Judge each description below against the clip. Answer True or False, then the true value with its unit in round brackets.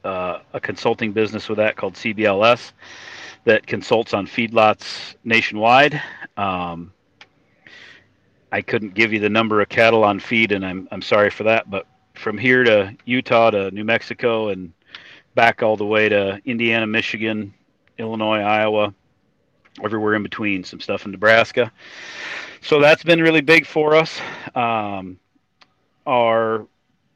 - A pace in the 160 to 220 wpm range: False (140 wpm)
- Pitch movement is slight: True (2.0 semitones)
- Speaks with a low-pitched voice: True (110 Hz)